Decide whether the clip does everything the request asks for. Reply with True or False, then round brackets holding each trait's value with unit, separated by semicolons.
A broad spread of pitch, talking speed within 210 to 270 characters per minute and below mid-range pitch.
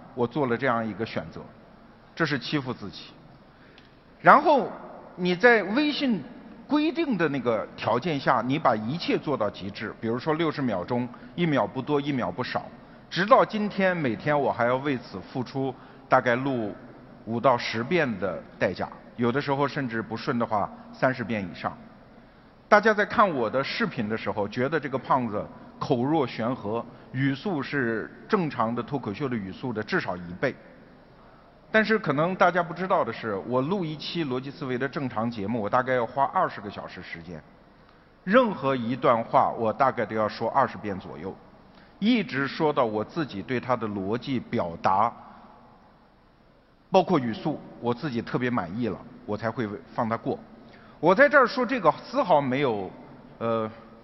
True (6.4 semitones; 250 characters per minute; 130 Hz)